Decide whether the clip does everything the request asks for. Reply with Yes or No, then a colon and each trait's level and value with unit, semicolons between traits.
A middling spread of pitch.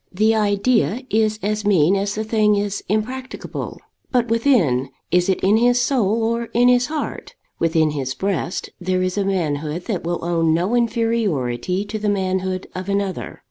Yes: average, 3.8 semitones